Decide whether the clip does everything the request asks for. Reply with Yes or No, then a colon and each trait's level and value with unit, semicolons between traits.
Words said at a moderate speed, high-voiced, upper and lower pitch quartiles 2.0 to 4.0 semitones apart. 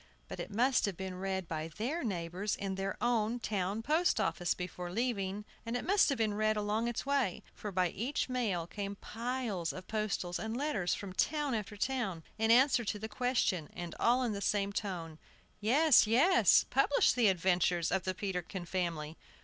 No: average, 180 wpm; high, 210 Hz; average, 4.7 semitones